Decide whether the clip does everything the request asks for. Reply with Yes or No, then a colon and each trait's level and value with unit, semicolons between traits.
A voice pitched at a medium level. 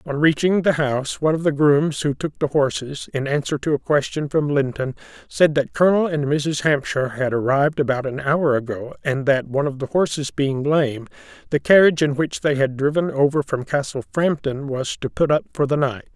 Yes: medium, 145 Hz